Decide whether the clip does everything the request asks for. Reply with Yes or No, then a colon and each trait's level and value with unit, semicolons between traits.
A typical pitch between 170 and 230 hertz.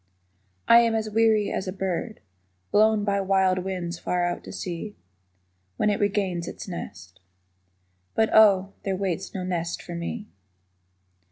Yes: high, 190 Hz